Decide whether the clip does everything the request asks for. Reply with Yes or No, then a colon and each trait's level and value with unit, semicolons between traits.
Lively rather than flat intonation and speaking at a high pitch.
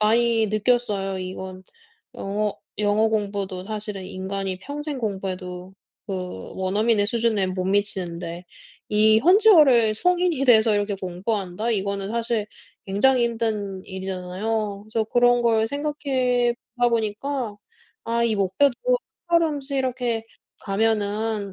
No: average, 3.5 semitones; high, 215 Hz